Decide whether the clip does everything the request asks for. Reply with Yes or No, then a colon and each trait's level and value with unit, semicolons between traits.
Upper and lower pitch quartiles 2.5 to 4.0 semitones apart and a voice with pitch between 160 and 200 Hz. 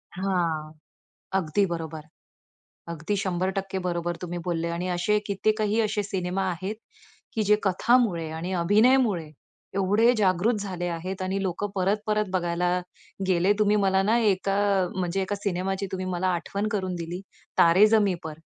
Yes: average, 2.9 semitones; high, 190 Hz